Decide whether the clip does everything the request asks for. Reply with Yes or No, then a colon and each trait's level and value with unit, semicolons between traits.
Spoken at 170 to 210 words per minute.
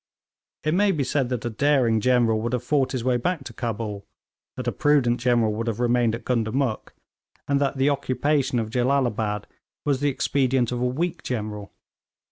Yes: average, 185 wpm